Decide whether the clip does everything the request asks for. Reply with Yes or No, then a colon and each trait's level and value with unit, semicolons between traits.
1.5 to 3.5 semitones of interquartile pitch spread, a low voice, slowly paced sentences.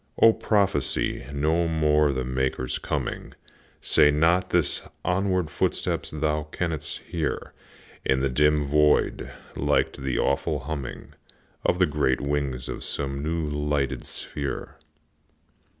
Yes: average, 2.7 semitones; very low, 75 Hz; slow, 125 wpm